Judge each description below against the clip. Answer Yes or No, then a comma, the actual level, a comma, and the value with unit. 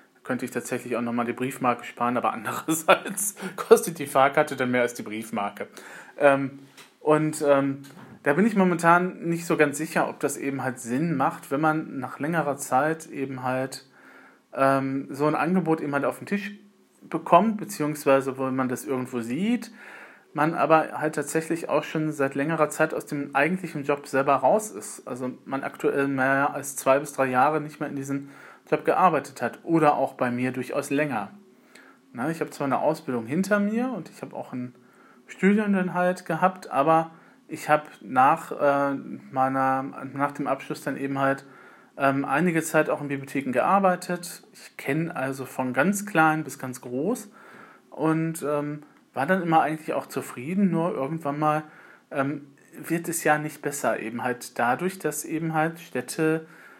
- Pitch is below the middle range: No, medium, 150 Hz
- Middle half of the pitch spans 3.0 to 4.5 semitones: Yes, average, 3.4 semitones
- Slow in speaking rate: No, average, 170 wpm